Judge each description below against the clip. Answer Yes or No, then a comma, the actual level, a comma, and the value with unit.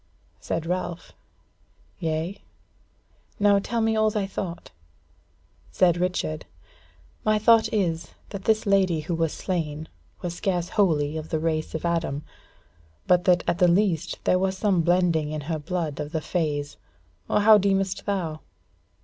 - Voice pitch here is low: No, medium, 175 Hz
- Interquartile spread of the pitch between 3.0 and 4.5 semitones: Yes, average, 3.5 semitones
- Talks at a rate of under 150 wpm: No, average, 155 wpm